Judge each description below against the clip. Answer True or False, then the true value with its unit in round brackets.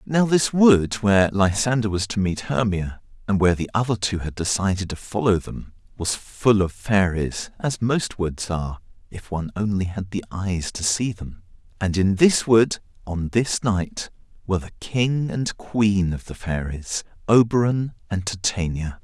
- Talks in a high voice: False (100 Hz)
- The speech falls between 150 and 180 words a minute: True (170 wpm)